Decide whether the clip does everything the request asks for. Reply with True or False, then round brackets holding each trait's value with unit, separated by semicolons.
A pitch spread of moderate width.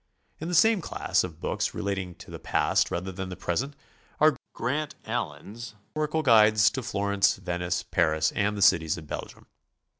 False (6.6 semitones)